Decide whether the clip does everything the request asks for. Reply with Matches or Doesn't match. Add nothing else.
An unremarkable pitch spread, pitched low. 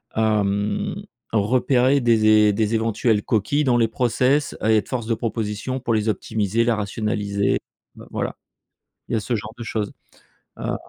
Doesn't match